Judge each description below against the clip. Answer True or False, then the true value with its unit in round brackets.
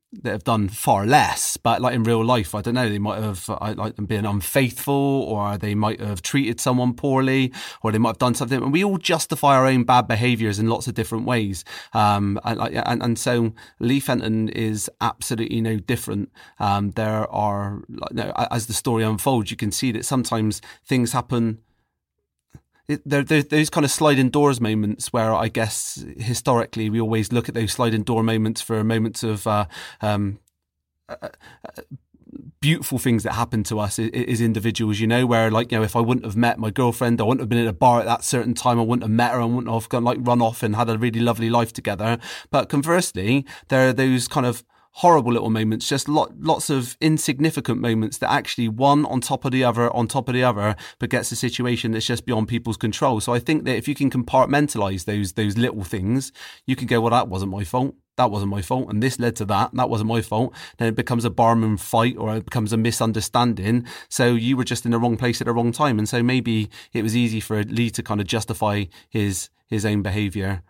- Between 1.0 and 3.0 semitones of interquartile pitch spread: True (2.5 semitones)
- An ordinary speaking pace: False (220 wpm)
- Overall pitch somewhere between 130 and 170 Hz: False (115 Hz)